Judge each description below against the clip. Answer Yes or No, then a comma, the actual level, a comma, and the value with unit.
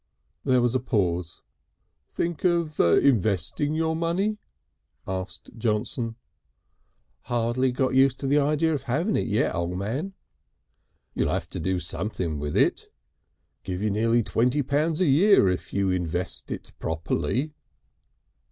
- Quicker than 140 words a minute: No, slow, 135 wpm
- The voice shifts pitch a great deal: Yes, wide, 8.0 semitones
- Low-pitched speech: Yes, low, 120 Hz